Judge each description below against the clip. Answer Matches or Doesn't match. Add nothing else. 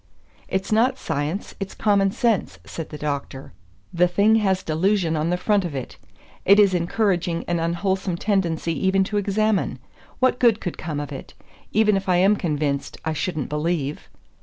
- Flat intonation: Doesn't match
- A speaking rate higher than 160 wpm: Matches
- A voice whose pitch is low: Doesn't match